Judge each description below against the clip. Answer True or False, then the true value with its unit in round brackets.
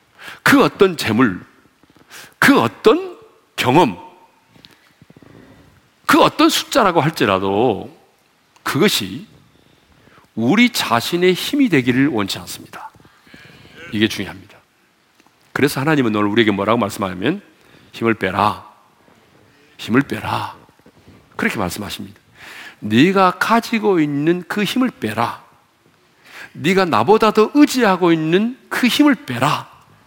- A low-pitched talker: False (165 Hz)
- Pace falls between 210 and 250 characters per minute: True (225 characters per minute)